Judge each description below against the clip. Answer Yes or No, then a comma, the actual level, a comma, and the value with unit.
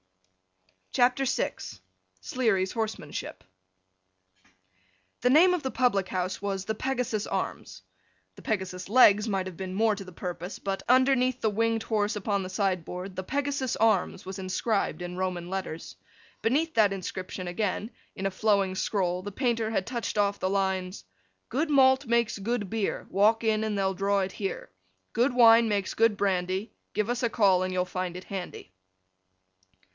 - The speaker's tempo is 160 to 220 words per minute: Yes, average, 165 wpm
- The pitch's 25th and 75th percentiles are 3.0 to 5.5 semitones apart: Yes, average, 3.6 semitones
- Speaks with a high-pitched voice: Yes, high, 205 Hz